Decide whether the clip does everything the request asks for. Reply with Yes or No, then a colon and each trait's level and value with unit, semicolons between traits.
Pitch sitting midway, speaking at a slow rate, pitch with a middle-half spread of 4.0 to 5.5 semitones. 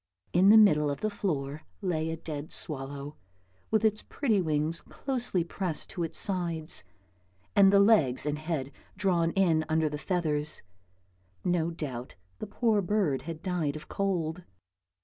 No: medium, 165 Hz; average, 150 wpm; average, 4.4 semitones